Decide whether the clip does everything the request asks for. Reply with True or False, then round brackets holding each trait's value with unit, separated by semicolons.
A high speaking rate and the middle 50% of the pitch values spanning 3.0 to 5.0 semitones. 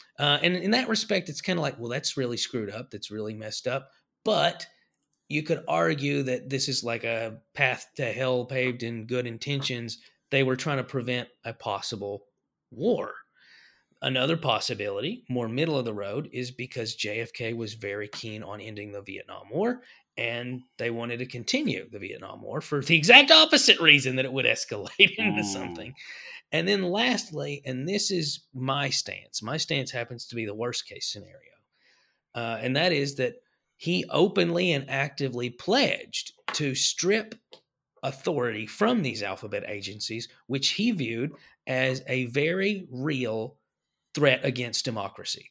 False (160 wpm; 4.5 semitones)